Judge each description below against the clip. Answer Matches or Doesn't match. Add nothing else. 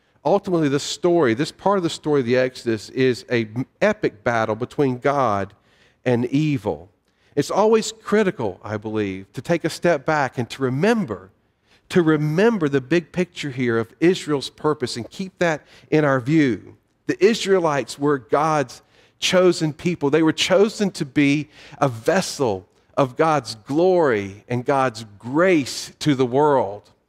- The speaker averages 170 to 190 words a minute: Doesn't match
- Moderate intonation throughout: Doesn't match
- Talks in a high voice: Doesn't match